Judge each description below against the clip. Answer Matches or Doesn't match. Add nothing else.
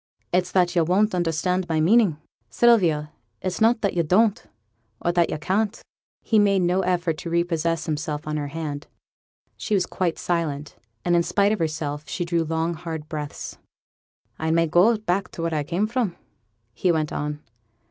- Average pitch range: Matches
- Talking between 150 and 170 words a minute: Doesn't match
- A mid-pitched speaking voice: Matches